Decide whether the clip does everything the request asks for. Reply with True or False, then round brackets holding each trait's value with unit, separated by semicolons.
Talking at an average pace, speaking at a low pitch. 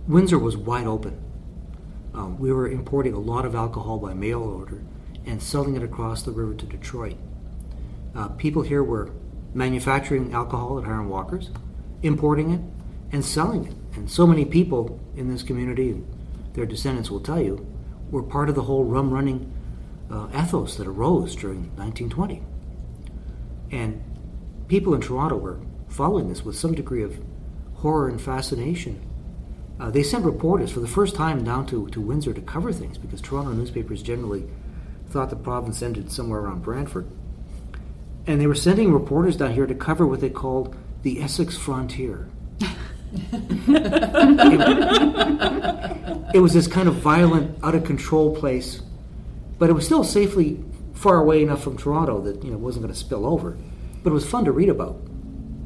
True (165 wpm; 125 Hz)